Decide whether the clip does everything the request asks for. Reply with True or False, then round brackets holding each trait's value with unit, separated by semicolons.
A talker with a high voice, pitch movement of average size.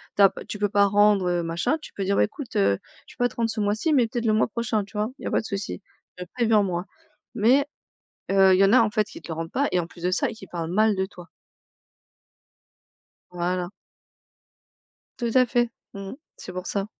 True (200 Hz; 3.5 semitones)